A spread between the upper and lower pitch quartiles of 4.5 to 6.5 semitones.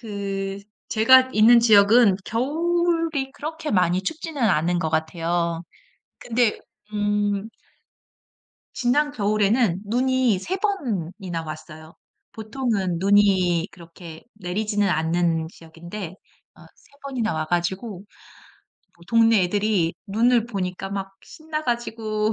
Yes: average, 5.3 semitones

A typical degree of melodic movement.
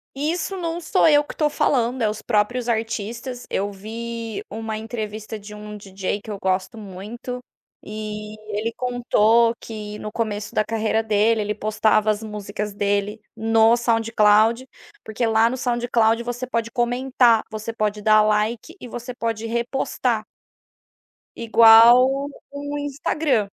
No: narrow, 2.3 semitones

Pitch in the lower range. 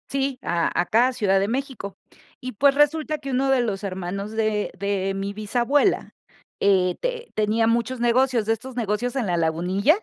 No: high, 225 Hz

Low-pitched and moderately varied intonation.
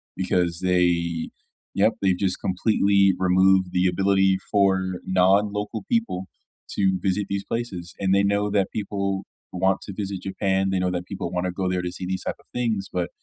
No: very low, 95 Hz; narrow, 1.5 semitones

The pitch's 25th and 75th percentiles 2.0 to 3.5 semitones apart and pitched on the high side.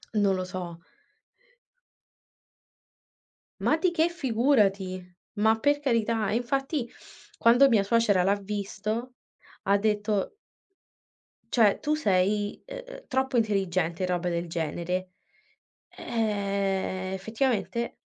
No: average, 4.2 semitones; high, 210 Hz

